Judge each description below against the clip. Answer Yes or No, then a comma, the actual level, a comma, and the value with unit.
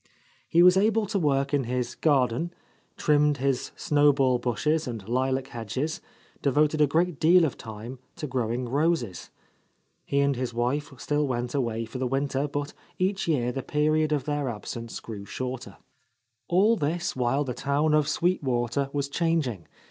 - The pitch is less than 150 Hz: Yes, medium, 140 Hz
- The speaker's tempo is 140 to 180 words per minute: Yes, average, 165 wpm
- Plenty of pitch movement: No, average, 3.6 semitones